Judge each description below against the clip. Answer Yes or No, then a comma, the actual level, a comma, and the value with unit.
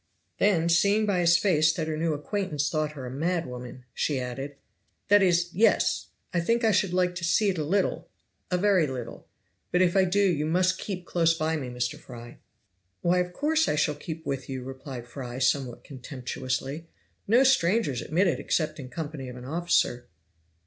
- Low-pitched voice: No, medium, 160 Hz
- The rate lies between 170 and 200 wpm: Yes, average, 185 wpm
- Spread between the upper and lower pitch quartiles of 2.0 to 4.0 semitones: No, average, 5.3 semitones